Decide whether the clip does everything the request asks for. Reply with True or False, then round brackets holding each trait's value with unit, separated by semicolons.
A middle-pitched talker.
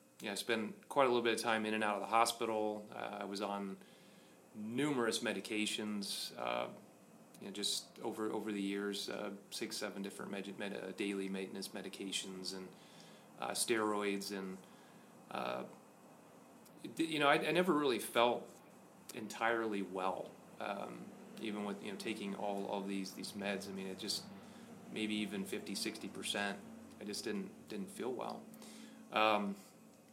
False (105 Hz)